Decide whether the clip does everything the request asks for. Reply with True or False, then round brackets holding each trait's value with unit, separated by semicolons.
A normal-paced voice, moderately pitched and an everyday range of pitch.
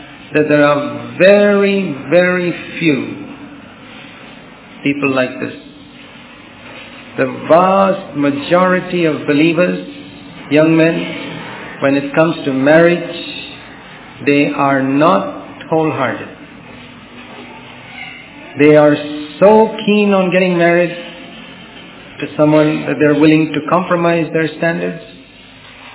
False (95 wpm; 160 Hz; 4.0 semitones)